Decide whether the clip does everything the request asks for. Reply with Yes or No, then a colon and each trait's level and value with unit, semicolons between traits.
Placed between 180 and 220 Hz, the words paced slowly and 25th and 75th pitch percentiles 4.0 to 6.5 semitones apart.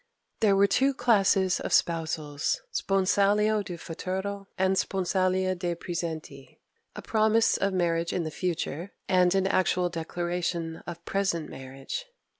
No: medium, 185 Hz; slow, 130 wpm; average, 2.7 semitones